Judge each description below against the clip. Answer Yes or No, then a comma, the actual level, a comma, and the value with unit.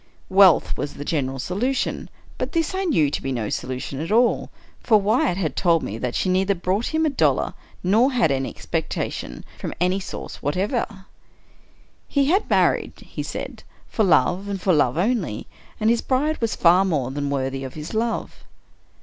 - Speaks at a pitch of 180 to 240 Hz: Yes, medium, 185 Hz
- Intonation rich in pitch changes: Yes, wide, 8.0 semitones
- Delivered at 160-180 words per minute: No, average, 190 wpm